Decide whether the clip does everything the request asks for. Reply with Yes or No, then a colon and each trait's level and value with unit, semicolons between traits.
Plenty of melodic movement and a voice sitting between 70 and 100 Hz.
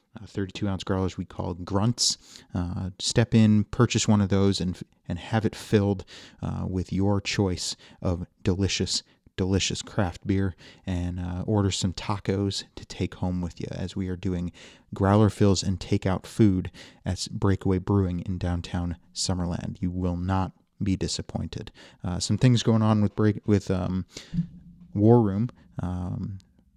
No: average, 2.8 semitones; very low, 95 Hz